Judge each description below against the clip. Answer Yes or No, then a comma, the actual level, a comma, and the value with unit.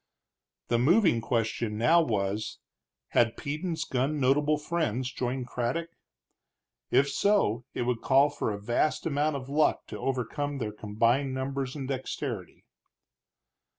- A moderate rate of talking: No, slow, 130 wpm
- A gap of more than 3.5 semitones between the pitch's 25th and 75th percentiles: Yes, average, 3.9 semitones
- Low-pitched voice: Yes, low, 130 Hz